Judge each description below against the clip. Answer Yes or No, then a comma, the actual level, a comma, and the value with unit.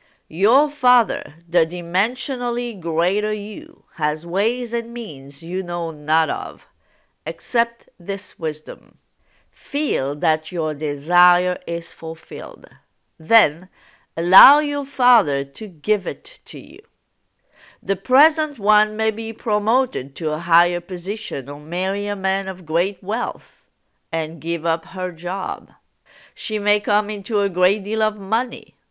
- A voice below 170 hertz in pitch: No, high, 190 Hz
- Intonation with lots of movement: No, average, 4.8 semitones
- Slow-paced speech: Yes, slow, 130 wpm